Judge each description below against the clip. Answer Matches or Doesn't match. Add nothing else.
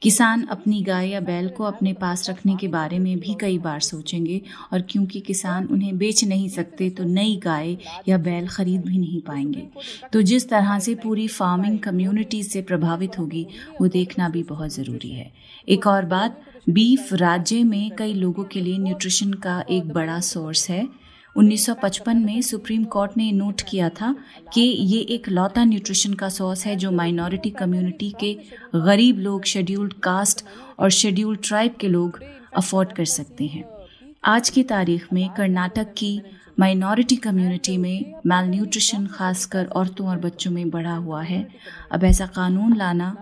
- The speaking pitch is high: Matches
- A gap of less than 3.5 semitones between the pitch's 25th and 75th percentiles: Matches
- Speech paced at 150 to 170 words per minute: Matches